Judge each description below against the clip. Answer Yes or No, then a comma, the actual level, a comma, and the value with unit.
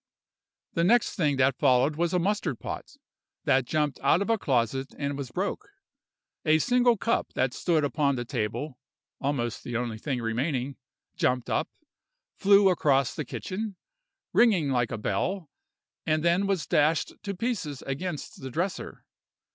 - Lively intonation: Yes, wide, 5.9 semitones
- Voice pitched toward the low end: No, medium, 150 Hz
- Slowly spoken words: No, average, 155 wpm